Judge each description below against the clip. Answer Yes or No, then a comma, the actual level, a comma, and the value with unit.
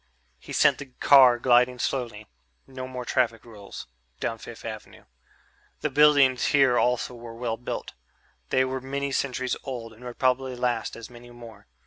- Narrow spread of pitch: Yes, narrow, 2.0 semitones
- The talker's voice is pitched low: Yes, low, 125 Hz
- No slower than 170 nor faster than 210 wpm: No, average, 160 wpm